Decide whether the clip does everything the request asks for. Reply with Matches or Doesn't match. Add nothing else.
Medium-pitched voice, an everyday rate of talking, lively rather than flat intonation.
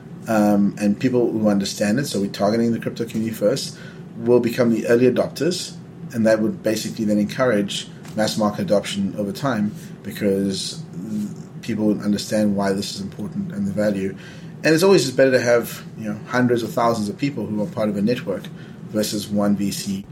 Doesn't match